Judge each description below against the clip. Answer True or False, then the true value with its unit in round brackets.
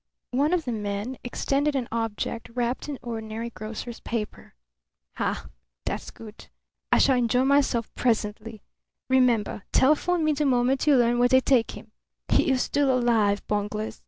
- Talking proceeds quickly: False (155 wpm)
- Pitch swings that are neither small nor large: True (3.1 semitones)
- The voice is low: False (240 Hz)